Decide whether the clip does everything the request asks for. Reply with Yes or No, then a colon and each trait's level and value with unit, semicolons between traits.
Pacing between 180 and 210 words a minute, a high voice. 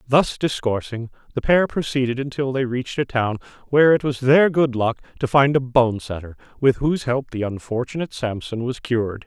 No: average, 190 wpm; low, 130 Hz